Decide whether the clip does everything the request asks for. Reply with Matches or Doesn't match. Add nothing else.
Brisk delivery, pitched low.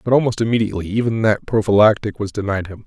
Doesn't match